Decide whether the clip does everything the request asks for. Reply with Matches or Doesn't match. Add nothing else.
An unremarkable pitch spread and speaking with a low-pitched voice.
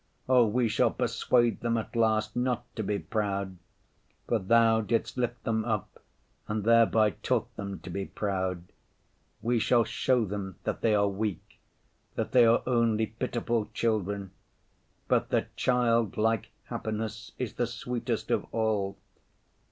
Doesn't match